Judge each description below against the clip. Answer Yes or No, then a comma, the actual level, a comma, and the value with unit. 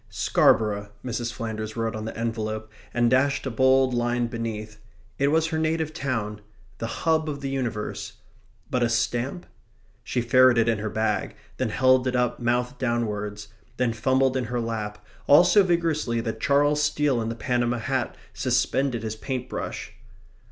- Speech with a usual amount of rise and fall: Yes, average, 3.0 semitones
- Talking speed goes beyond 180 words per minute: No, average, 165 wpm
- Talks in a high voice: No, low, 120 Hz